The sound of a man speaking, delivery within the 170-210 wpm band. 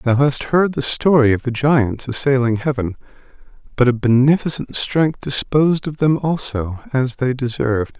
No: male; average, 160 wpm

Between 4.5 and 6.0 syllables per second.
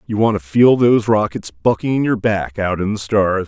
Yes: 5.0 syllables/s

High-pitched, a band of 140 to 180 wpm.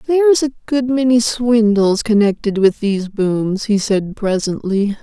Yes: high, 220 Hz; average, 145 wpm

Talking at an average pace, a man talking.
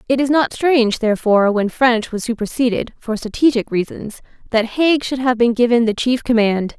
No: average, 185 wpm; female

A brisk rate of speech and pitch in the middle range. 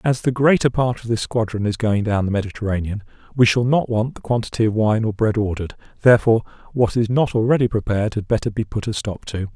No: fast, 225 wpm; low, 110 Hz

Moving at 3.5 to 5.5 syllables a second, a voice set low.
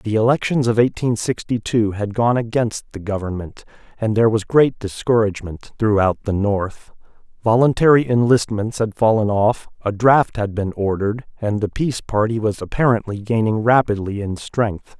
Yes: 5.0 syllables/s; low, 110 Hz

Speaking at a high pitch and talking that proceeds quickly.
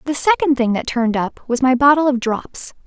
Yes: very high, 260 Hz; fast, 230 wpm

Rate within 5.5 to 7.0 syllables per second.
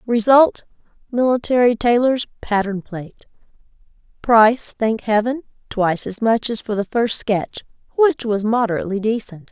No: 4.9 syllables/s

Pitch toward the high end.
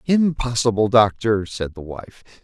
No: low, 110 Hz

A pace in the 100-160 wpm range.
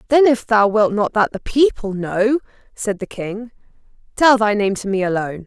No: average, 200 wpm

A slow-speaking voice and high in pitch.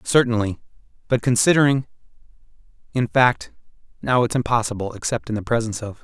No: slow, 130 wpm; low, 120 Hz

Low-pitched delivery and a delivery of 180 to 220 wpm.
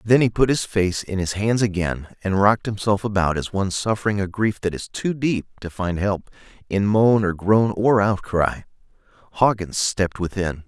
Yes: low, 100 Hz; average, 190 wpm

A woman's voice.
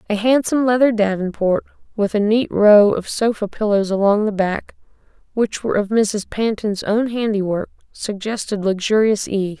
Yes: female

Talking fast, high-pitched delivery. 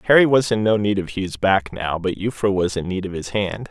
No: fast, 275 wpm; low, 100 Hz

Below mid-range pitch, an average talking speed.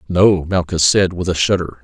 Yes: very low, 90 Hz; average, 195 wpm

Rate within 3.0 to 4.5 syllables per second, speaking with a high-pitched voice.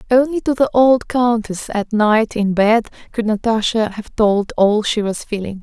Yes: 4.3 syllables/s; high, 220 Hz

